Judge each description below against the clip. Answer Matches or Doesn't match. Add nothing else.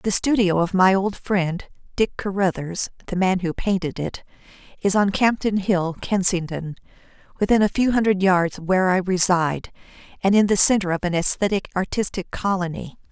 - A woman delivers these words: Matches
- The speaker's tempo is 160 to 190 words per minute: Matches